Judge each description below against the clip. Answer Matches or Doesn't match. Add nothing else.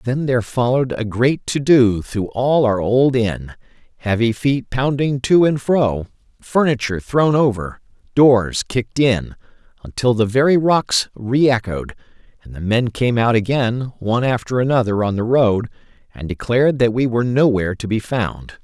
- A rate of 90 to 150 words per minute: Doesn't match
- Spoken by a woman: Doesn't match